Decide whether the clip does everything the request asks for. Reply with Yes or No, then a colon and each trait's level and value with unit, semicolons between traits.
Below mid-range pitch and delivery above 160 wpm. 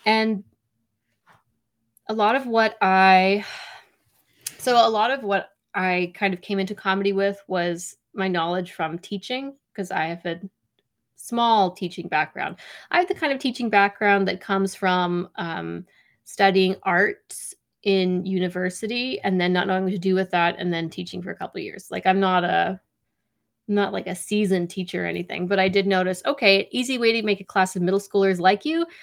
No: high, 190 Hz; average, 185 wpm